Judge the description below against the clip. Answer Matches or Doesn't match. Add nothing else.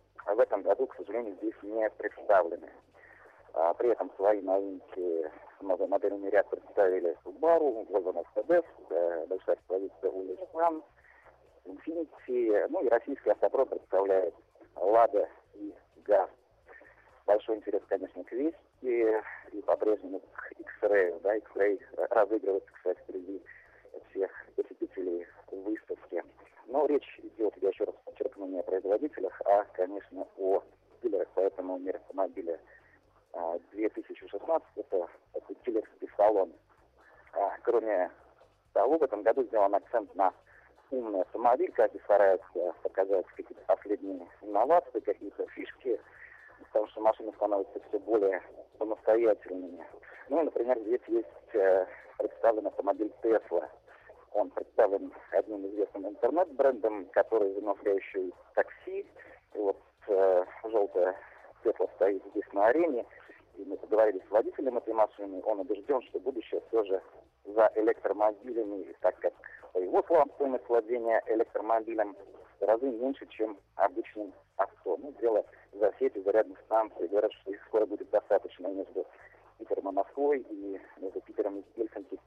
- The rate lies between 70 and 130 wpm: Matches